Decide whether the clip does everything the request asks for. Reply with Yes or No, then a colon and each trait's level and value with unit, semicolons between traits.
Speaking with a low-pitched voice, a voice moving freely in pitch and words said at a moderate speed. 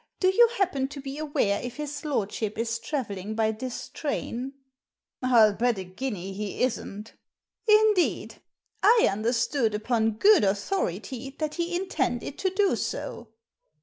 No: very high, 250 Hz; wide, 6.1 semitones; average, 150 wpm